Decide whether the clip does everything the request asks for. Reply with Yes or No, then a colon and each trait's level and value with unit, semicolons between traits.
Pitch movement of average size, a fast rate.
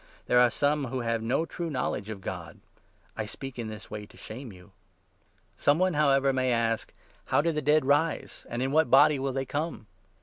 Yes: average, 4.3 semitones; fast, 210 wpm